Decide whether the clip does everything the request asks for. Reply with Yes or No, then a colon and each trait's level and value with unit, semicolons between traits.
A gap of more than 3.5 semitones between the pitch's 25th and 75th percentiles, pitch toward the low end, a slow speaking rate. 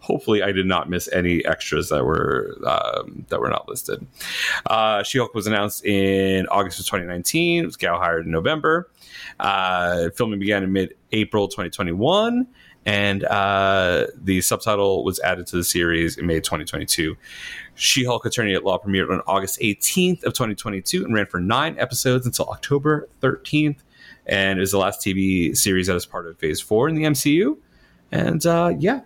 No: wide, 5.5 semitones; low, 100 Hz; average, 190 wpm